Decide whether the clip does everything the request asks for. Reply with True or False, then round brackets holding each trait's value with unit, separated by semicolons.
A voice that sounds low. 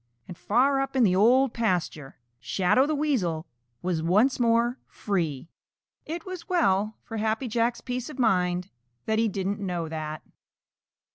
False (220 Hz)